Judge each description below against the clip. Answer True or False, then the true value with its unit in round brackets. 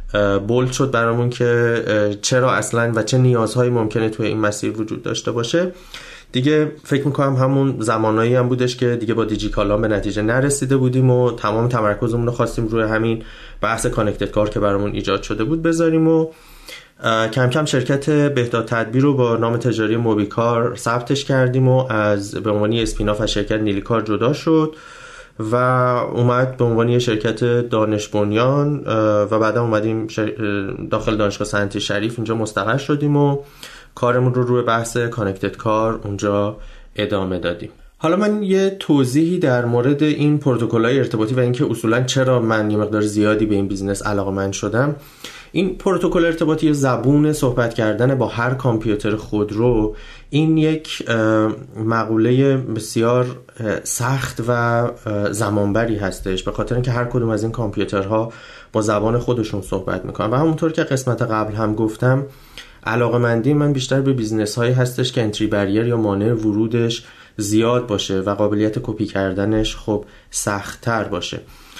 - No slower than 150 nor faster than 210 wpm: True (155 wpm)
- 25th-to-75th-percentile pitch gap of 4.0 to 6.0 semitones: False (3.2 semitones)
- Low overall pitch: True (115 Hz)